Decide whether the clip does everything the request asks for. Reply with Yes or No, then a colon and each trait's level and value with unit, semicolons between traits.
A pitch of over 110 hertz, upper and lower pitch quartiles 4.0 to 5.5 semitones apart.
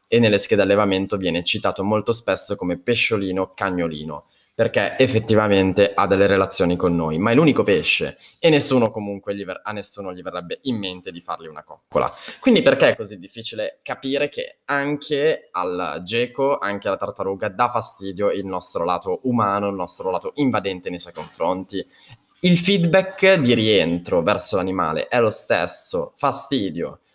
No: low, 100 Hz; average, 4.5 semitones